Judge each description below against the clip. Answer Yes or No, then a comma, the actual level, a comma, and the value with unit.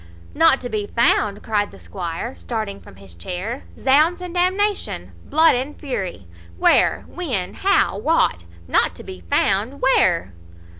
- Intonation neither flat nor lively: No, wide, 9.0 semitones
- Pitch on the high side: Yes, high, 235 Hz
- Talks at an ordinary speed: Yes, average, 150 wpm